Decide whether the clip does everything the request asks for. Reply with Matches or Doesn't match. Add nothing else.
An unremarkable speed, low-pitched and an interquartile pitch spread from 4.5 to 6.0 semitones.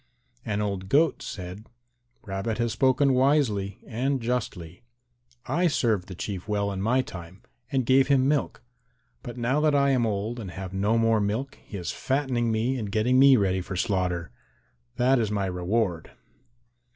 Matches